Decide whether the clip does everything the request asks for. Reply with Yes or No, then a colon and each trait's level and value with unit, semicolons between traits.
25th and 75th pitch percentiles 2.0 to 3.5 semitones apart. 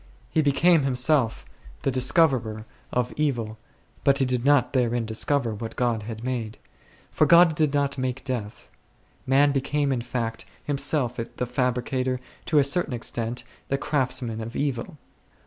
Yes: average, 3.2 semitones